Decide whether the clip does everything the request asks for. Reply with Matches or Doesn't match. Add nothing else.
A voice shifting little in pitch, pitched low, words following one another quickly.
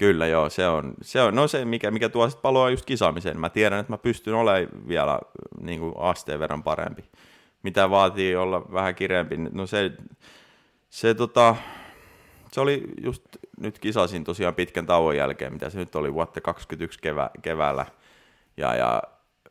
Doesn't match